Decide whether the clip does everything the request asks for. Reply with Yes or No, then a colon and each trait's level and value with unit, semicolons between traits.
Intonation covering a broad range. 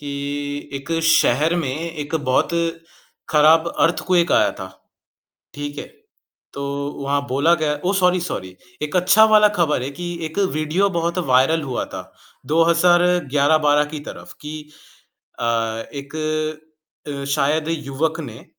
No: average, 3.2 semitones